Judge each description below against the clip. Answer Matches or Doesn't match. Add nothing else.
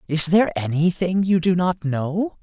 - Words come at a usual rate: Matches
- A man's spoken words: Matches